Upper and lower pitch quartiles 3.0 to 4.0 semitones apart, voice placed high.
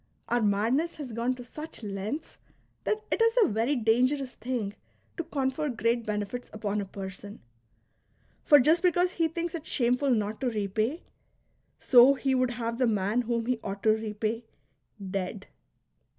No: average, 4.6 semitones; high, 240 Hz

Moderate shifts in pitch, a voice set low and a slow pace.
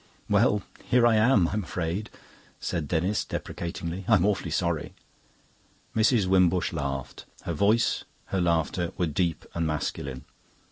Yes: average, 4.0 semitones; very low, 90 Hz; slow, 130 wpm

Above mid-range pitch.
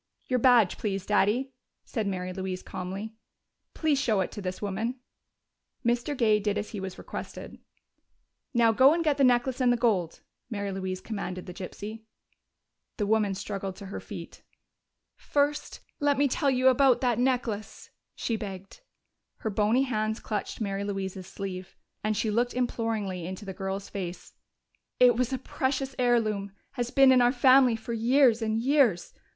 Yes: high, 220 Hz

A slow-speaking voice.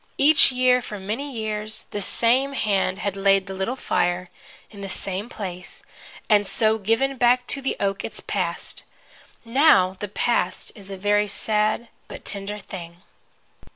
No: average, 155 wpm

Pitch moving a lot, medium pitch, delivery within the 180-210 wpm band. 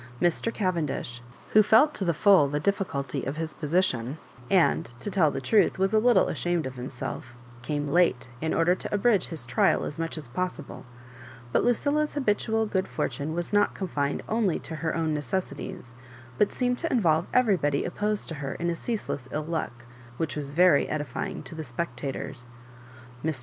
Yes: wide, 5.8 semitones; medium, 165 Hz; average, 185 wpm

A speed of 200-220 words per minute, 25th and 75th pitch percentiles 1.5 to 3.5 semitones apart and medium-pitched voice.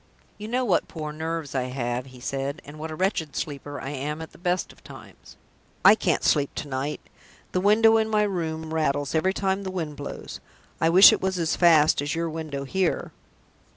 No: fast, 205 wpm; average, 4.4 semitones; medium, 160 Hz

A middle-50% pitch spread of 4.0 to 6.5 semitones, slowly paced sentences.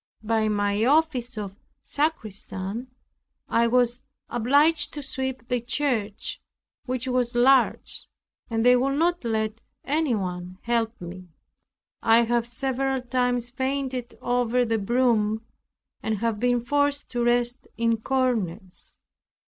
No: average, 2.9 semitones; slow, 120 wpm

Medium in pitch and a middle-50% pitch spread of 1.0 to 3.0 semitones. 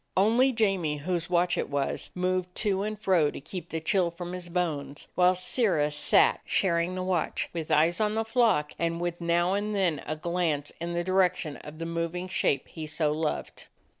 Yes: medium, 175 Hz; narrow, 2.6 semitones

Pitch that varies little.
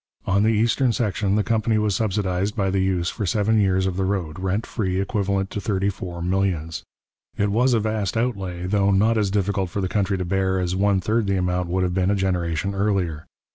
Yes: narrow, 2.1 semitones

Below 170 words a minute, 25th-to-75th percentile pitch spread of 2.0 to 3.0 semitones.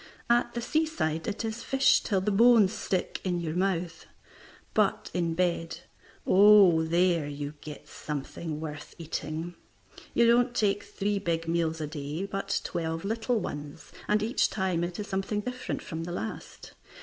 No: average, 160 wpm; average, 4.4 semitones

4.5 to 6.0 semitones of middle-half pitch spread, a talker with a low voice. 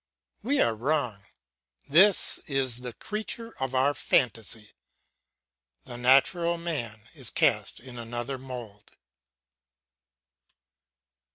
Yes: average, 5.0 semitones; low, 130 Hz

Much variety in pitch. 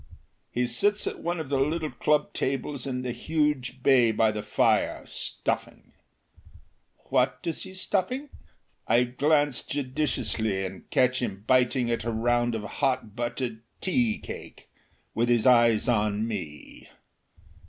No: average, 3.8 semitones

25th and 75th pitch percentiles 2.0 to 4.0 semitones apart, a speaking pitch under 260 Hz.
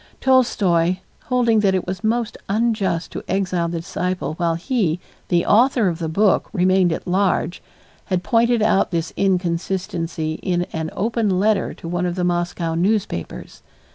Yes: average, 3.7 semitones; medium, 185 Hz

